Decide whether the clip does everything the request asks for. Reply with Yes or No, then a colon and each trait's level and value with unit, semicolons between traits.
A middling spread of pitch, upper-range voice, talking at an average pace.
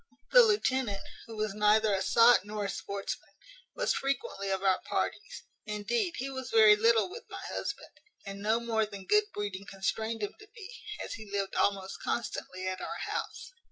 Yes: average, 3.8 semitones; high, 215 Hz; average, 180 wpm